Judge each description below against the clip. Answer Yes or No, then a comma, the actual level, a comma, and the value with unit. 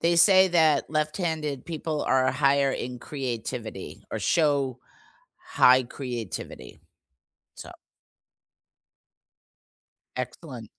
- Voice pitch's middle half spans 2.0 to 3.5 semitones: No, average, 4.1 semitones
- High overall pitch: No, medium, 140 Hz